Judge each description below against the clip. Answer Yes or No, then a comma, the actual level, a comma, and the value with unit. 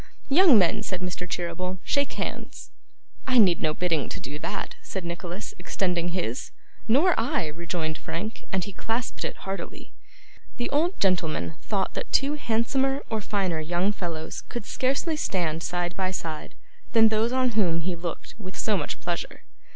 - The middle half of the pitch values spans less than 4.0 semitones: No, average, 4.9 semitones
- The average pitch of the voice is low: No, medium, 185 Hz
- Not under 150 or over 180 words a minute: Yes, average, 165 wpm